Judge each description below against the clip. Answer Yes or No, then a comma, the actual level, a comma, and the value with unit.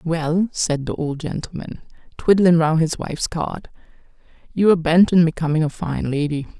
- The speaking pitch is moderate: Yes, medium, 165 Hz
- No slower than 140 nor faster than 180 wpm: Yes, average, 165 wpm